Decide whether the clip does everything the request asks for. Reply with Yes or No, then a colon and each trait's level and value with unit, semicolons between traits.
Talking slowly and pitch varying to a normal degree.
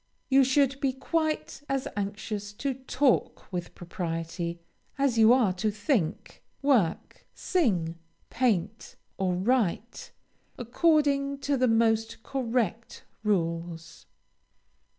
No: slow, 105 wpm; wide, 6.5 semitones